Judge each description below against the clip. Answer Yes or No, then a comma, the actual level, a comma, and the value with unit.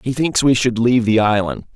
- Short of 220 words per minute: No, fast, 240 wpm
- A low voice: Yes, low, 115 Hz